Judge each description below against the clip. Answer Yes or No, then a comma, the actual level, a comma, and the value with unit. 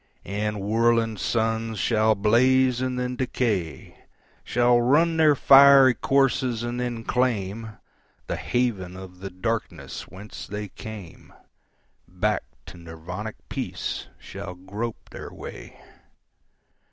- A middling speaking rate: No, slow, 105 wpm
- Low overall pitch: Yes, low, 115 Hz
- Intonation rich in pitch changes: No, average, 3.8 semitones